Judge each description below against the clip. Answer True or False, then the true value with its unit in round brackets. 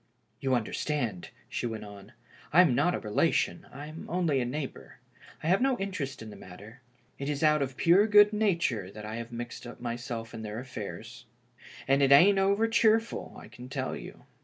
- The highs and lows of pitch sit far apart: True (7.0 semitones)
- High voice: False (135 Hz)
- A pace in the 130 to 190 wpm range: False (200 wpm)